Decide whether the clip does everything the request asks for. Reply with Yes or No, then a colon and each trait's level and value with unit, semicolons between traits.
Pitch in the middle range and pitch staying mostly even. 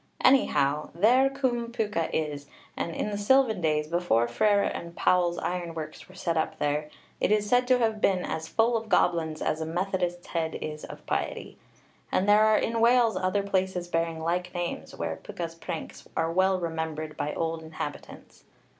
No: medium, 175 Hz; average, 4.6 semitones